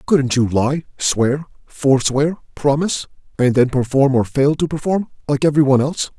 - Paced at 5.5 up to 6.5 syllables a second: No, 4.9 syllables/s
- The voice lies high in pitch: No, medium, 140 Hz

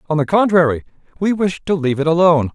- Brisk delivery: Yes, fast, 210 wpm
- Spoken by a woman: No, male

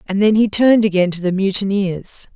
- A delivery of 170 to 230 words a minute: Yes, fast, 205 wpm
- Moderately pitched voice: No, high, 200 Hz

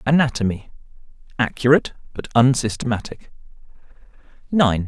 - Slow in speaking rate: Yes, slow, 50 wpm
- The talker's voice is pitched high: No, low, 125 Hz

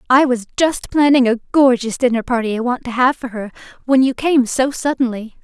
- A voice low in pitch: No, very high, 250 Hz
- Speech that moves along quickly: Yes, fast, 210 wpm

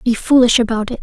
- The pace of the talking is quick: Yes, fast, 235 wpm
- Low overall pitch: No, high, 235 Hz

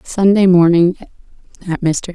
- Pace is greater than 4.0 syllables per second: No, 3.8 syllables/s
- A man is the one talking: No, female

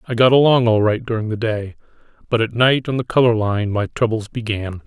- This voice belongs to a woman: No, male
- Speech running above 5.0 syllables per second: Yes, 5.5 syllables/s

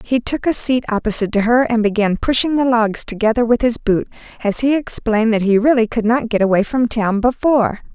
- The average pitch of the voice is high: Yes, high, 230 Hz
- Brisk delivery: Yes, fast, 220 wpm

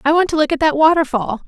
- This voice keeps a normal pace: No, fast, 285 wpm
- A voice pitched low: No, very high, 300 Hz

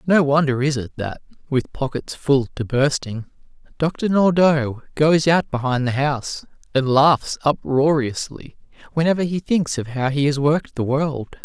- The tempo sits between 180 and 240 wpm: No, average, 155 wpm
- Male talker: Yes, male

